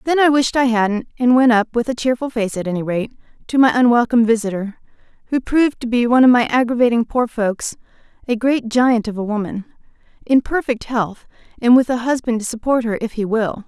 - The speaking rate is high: Yes, fast, 210 wpm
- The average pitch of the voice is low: No, high, 235 Hz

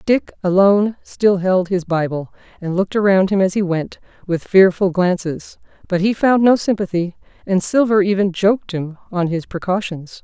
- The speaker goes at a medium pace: Yes, average, 170 wpm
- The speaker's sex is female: Yes, female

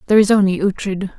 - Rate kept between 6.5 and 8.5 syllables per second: Yes, 6.9 syllables/s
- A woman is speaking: Yes, female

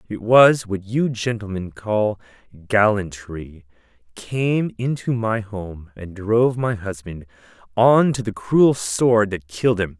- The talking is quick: No, average, 140 wpm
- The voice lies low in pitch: Yes, low, 105 Hz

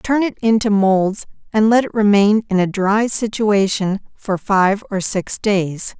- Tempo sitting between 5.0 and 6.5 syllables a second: No, 3.9 syllables/s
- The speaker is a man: No, female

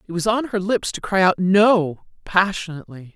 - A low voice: No, high, 190 Hz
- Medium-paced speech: Yes, average, 190 wpm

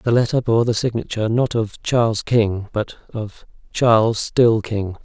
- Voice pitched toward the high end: No, low, 115 Hz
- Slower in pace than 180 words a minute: Yes, average, 155 wpm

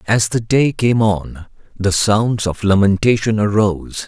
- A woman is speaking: No, male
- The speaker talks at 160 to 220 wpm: No, average, 145 wpm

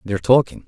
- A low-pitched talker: Yes, low, 105 Hz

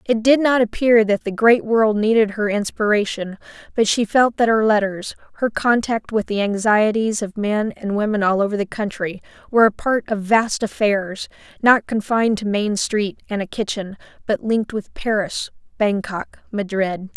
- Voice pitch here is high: Yes, high, 210 Hz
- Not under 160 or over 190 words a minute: Yes, average, 175 wpm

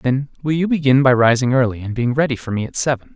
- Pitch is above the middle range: No, low, 130 Hz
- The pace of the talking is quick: Yes, fast, 265 wpm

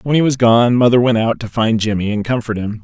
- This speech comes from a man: Yes, male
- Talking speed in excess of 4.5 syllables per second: Yes, 5.9 syllables/s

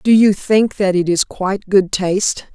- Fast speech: Yes, fast, 210 wpm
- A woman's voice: Yes, female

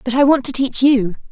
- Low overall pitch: No, very high, 255 Hz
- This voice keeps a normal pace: No, fast, 275 wpm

